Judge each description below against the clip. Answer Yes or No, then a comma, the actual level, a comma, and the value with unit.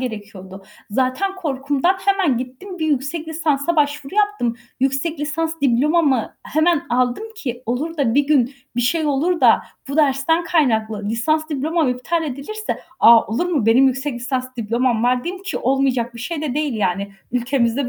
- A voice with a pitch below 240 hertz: No, very high, 275 Hz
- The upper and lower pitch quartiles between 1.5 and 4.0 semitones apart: No, average, 4.6 semitones